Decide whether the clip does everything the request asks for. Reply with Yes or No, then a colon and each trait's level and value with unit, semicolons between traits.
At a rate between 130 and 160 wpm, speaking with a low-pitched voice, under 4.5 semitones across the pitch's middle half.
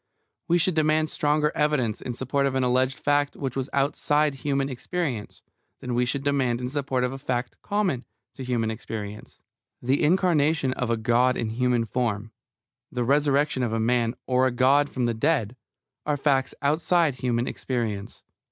No: average, 170 wpm; low, 130 Hz; average, 3.2 semitones